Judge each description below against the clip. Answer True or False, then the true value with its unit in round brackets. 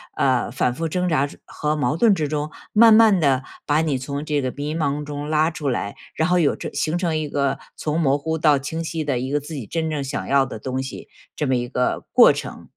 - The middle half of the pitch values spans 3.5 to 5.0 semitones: False (2.8 semitones)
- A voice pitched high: False (150 Hz)